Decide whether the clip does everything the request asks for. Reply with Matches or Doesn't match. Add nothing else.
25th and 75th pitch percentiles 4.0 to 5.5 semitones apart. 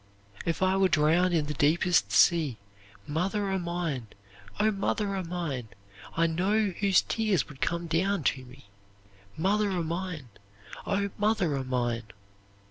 Matches